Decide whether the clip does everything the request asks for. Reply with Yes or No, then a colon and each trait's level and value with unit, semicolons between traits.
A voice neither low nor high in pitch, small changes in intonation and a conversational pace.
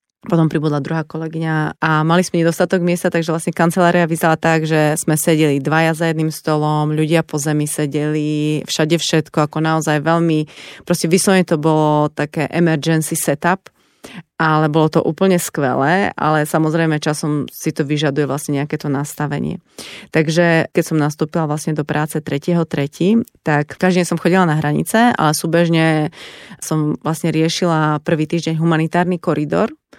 Yes: medium, 160 Hz; narrow, 1.8 semitones; average, 150 wpm